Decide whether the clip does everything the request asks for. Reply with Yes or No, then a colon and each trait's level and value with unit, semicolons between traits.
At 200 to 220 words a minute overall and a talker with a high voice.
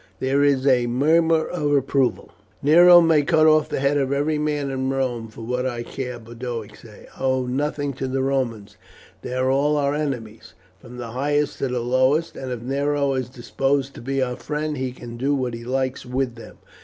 No: fast, 205 wpm; low, 135 Hz